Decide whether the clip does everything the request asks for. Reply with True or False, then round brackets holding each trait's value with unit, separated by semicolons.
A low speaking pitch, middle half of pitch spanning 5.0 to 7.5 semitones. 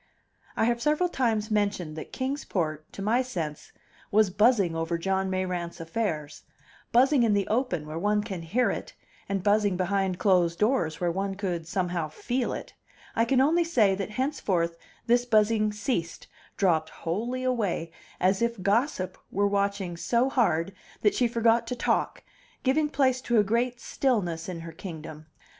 False (205 Hz; 5.4 semitones)